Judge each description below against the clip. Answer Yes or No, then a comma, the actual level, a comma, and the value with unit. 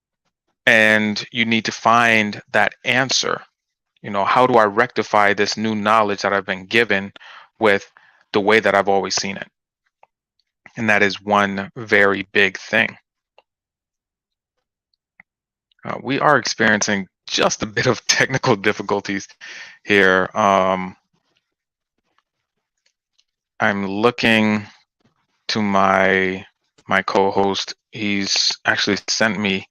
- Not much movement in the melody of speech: Yes, narrow, 1.8 semitones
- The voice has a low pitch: Yes, low, 100 Hz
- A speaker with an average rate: No, slow, 115 wpm